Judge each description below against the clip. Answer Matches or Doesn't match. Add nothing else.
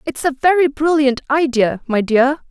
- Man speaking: Doesn't match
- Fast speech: Doesn't match